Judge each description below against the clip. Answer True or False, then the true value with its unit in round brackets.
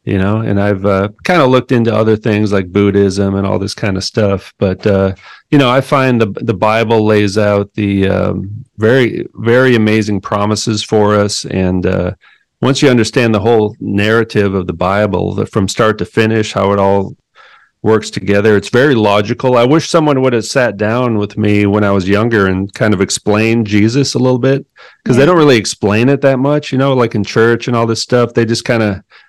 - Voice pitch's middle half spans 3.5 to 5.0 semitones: False (2.9 semitones)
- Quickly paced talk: True (215 wpm)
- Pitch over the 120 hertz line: False (110 Hz)